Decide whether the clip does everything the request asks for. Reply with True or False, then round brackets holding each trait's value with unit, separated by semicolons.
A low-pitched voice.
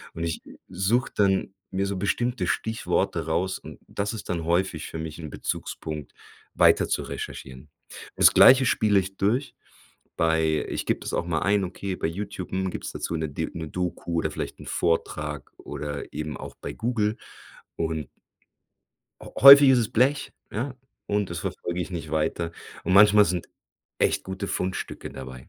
True (90 Hz)